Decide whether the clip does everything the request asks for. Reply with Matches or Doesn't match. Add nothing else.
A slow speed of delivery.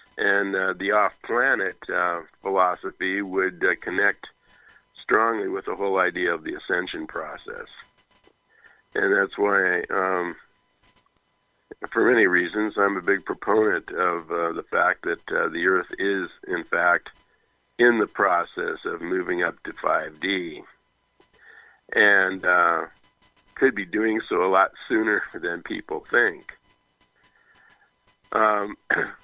Matches